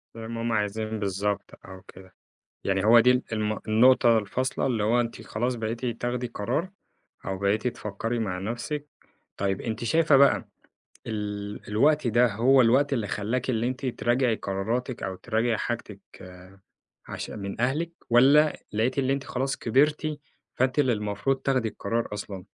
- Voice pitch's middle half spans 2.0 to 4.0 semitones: Yes, average, 3.6 semitones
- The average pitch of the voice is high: No, low, 115 Hz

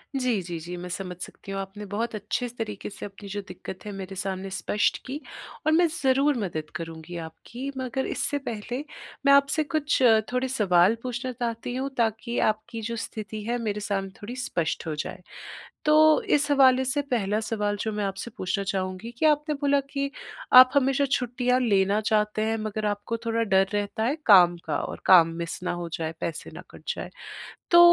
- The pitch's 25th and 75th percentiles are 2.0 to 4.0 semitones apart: No, average, 4.8 semitones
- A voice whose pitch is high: Yes, high, 215 Hz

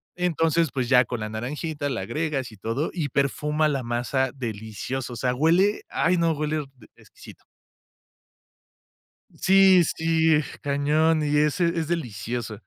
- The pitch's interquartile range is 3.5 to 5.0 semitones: Yes, average, 4.6 semitones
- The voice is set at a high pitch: No, medium, 145 Hz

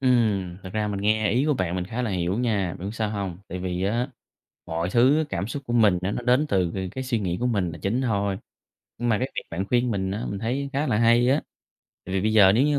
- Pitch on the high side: No, low, 105 Hz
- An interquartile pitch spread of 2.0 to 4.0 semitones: No, average, 4.5 semitones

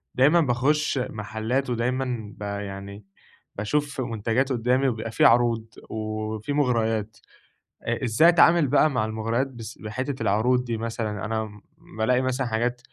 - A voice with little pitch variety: No, average, 3.0 semitones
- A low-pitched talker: Yes, low, 115 Hz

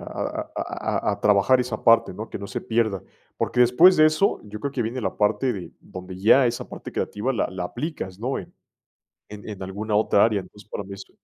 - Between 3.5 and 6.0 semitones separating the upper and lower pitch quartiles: Yes, average, 3.9 semitones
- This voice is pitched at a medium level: No, low, 110 Hz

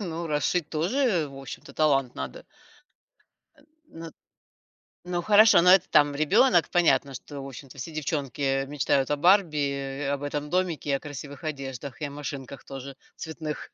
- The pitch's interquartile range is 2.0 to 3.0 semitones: No, average, 3.5 semitones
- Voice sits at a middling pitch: Yes, medium, 150 Hz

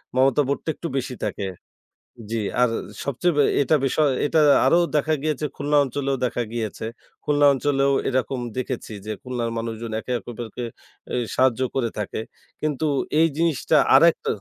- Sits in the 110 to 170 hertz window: Yes, low, 135 Hz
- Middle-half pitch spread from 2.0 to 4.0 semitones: Yes, average, 3.6 semitones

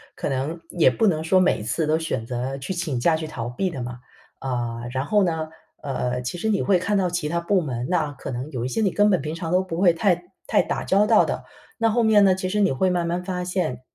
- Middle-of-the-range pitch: Yes, medium, 165 Hz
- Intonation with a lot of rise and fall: Yes, wide, 6.0 semitones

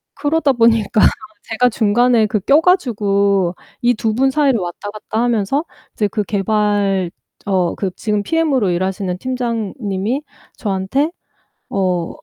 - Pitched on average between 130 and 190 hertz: No, high, 215 Hz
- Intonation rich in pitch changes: No, average, 4.1 semitones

